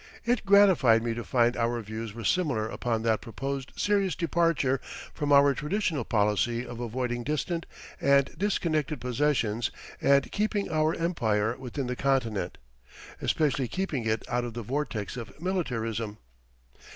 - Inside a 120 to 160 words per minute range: Yes, average, 140 wpm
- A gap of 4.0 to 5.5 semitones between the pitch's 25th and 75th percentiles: Yes, average, 5.2 semitones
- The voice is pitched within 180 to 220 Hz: No, low, 130 Hz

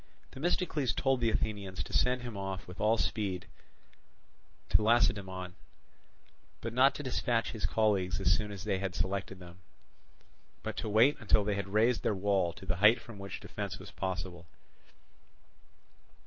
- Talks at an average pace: Yes, average, 160 wpm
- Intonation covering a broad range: No, average, 3.5 semitones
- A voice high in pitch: No, low, 105 Hz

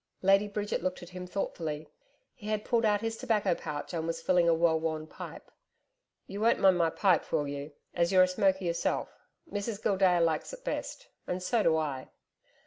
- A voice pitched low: No, medium, 180 Hz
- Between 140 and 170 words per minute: No, average, 195 wpm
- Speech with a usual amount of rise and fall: Yes, average, 3.9 semitones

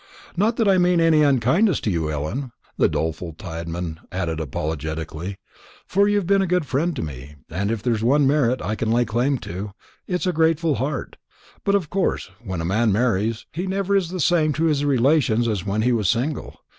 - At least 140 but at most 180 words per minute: No, average, 200 wpm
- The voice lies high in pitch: No, low, 125 Hz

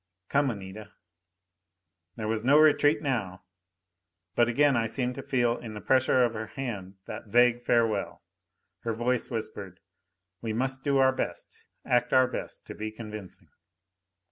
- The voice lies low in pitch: Yes, low, 120 Hz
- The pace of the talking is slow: No, average, 150 wpm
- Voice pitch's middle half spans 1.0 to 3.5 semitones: Yes, average, 3.2 semitones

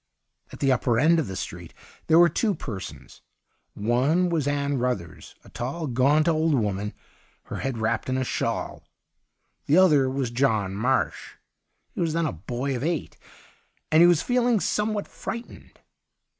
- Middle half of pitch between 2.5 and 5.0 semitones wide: No, wide, 5.6 semitones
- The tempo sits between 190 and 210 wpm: No, average, 165 wpm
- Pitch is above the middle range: No, low, 135 Hz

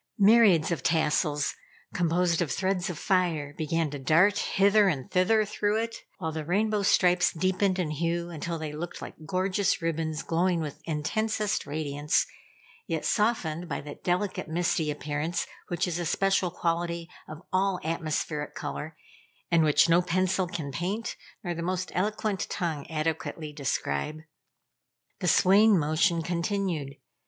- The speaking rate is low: No, average, 145 wpm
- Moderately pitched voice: Yes, medium, 170 Hz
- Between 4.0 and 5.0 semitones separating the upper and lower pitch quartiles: No, average, 3.2 semitones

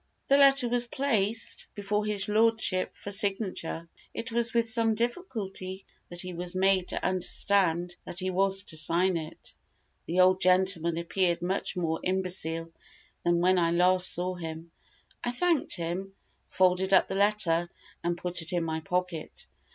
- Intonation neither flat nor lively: Yes, average, 3.0 semitones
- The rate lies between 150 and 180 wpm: Yes, average, 160 wpm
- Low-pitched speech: No, medium, 185 Hz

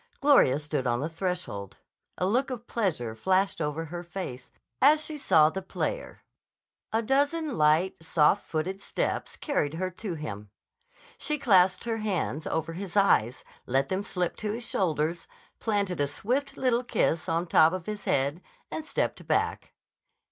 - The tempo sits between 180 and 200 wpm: No, average, 160 wpm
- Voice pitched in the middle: Yes, medium, 180 Hz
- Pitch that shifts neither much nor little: No, wide, 6.4 semitones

